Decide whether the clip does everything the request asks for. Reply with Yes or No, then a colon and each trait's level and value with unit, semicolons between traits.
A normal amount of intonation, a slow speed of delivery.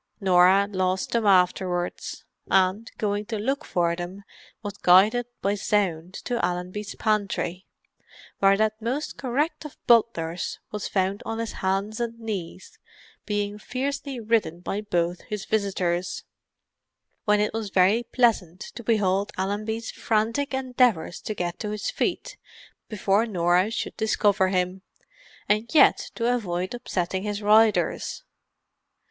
Yes: average, 3.3 semitones; slow, 130 wpm